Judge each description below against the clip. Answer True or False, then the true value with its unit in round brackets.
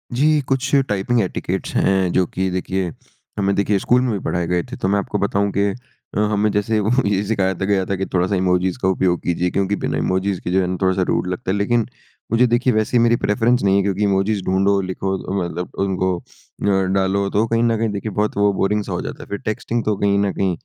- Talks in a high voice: False (100 Hz)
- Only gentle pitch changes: True (2.1 semitones)